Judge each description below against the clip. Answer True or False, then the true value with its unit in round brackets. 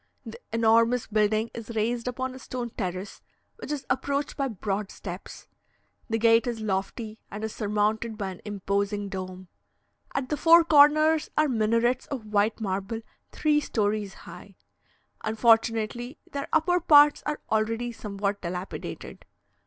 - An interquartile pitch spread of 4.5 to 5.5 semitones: False (3.8 semitones)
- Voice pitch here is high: True (225 Hz)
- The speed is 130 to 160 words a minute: True (140 wpm)